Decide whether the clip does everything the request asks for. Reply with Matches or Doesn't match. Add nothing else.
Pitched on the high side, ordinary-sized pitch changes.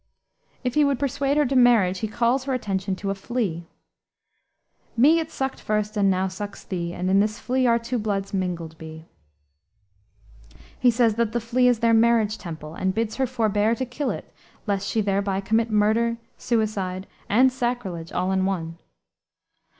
Matches